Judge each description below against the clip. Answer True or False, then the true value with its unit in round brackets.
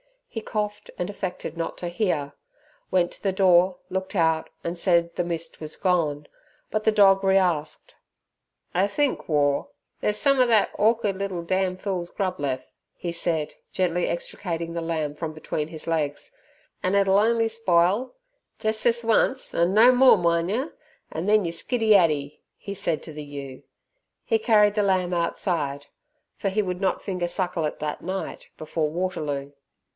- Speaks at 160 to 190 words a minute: True (170 wpm)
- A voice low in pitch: False (180 Hz)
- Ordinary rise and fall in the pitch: True (3.9 semitones)